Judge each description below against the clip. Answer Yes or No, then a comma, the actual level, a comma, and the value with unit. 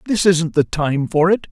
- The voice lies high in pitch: No, medium, 170 Hz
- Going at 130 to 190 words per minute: No, fast, 240 wpm